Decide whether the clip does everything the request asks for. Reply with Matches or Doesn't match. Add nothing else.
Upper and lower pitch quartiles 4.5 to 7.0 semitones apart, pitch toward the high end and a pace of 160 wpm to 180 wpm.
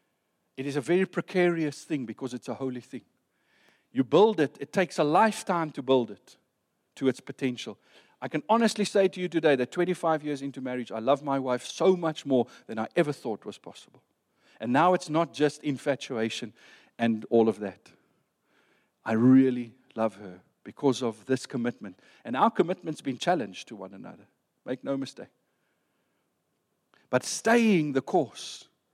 Doesn't match